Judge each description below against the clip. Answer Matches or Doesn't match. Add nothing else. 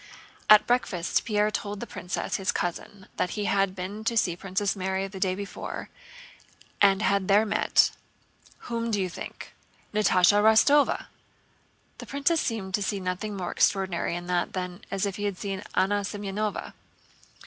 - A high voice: Matches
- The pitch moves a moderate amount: Doesn't match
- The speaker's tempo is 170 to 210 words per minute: Doesn't match